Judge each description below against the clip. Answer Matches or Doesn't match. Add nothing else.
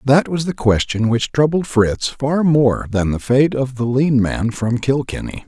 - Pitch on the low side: Matches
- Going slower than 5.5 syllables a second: Matches